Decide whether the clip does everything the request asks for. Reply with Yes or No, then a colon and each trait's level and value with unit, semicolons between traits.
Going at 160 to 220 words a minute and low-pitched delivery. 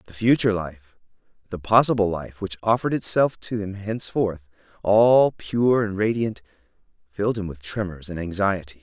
No: average, 150 wpm; low, 100 Hz